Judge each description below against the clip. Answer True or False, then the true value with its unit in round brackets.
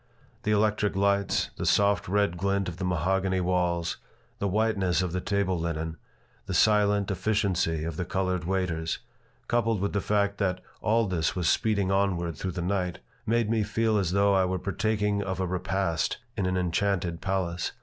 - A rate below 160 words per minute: False (175 wpm)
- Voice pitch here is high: False (95 Hz)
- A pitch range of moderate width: False (2.2 semitones)